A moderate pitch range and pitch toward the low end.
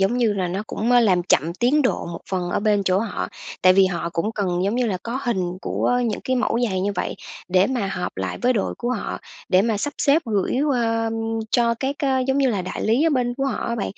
No: average, 4.7 semitones; high, 220 Hz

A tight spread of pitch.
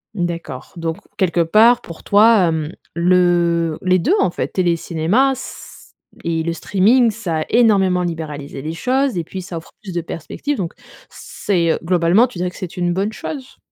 No: average, 3.7 semitones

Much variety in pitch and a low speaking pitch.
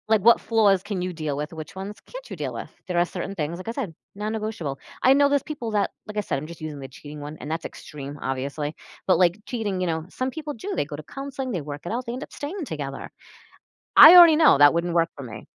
No: wide, 7.6 semitones; medium, 185 Hz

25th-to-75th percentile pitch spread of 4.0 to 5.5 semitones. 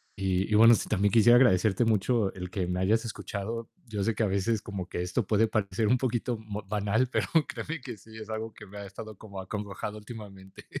No: narrow, 2.5 semitones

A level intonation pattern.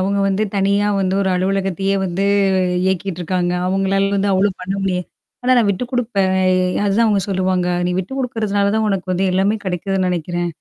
Yes: narrow, 1.5 semitones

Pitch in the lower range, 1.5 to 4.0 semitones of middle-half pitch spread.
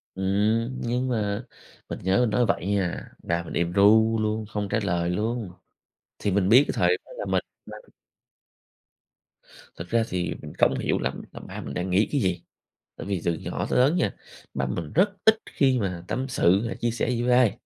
No: low, 105 Hz; average, 4.7 semitones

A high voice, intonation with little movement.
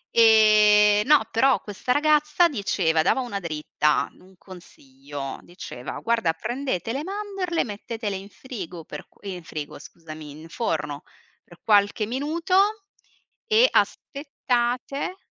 No: high, 215 Hz; wide, 8.3 semitones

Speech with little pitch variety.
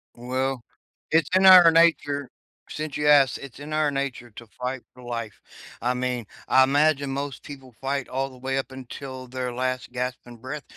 Yes: narrow, 2.3 semitones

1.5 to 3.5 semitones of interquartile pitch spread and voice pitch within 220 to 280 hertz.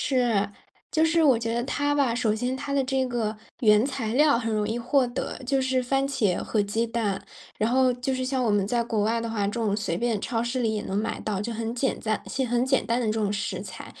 Yes: average, 3.2 semitones; high, 235 Hz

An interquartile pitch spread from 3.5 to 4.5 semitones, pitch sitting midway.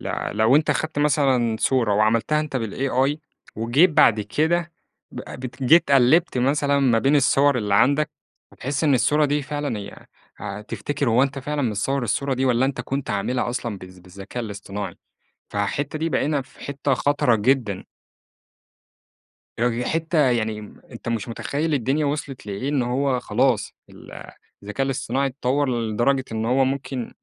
No: average, 3.9 semitones; low, 130 Hz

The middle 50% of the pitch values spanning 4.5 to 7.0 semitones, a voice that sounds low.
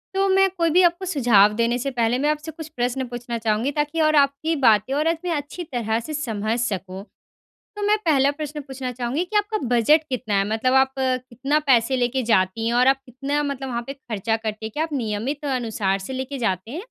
No: average, 4.8 semitones; very high, 255 Hz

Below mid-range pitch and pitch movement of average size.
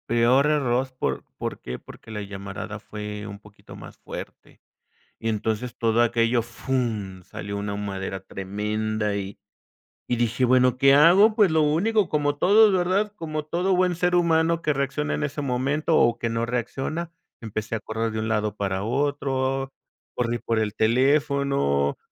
No: low, 120 Hz; wide, 5.7 semitones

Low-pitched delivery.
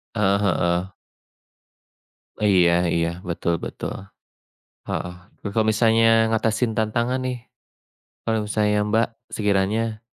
Yes: low, 105 Hz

